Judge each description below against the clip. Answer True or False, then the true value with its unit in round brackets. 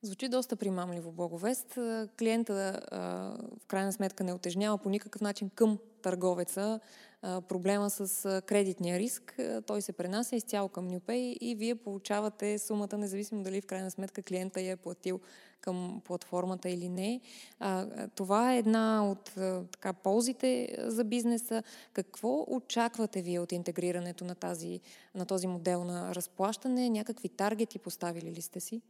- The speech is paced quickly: False (140 wpm)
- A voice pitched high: True (200 Hz)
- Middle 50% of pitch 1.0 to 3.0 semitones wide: False (3.5 semitones)